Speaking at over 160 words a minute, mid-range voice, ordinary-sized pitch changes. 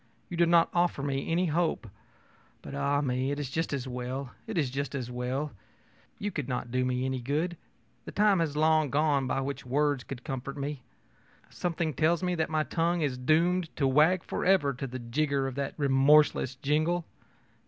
Yes: average, 190 wpm; medium, 145 Hz; average, 3.6 semitones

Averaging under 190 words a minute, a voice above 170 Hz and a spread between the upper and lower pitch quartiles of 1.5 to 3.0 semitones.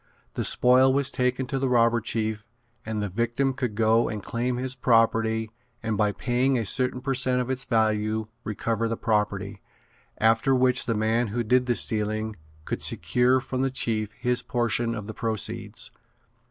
No: average, 175 wpm; low, 115 Hz; narrow, 2.5 semitones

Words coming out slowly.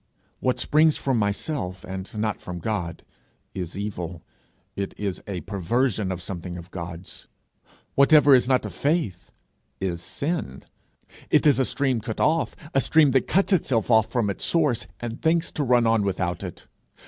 No: average, 165 wpm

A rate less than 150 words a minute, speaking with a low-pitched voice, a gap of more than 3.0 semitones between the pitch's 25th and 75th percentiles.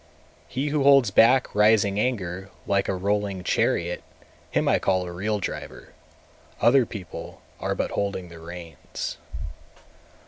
Yes: average, 140 wpm; low, 100 Hz; average, 3.8 semitones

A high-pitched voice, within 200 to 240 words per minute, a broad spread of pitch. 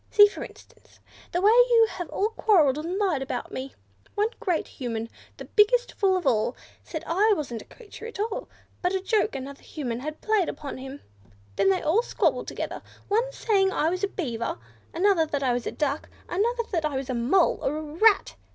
Yes: very high, 350 Hz; fast, 205 wpm; wide, 7.4 semitones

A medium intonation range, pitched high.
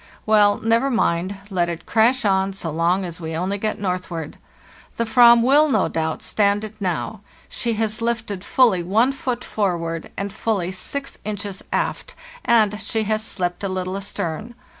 Yes: average, 3.8 semitones; high, 205 Hz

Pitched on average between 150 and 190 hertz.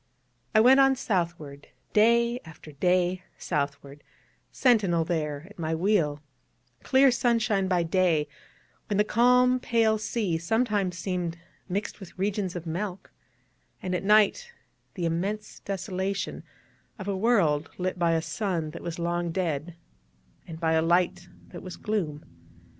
Yes: medium, 185 Hz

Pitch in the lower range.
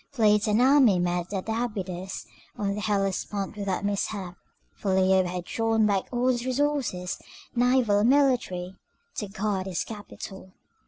No: high, 205 Hz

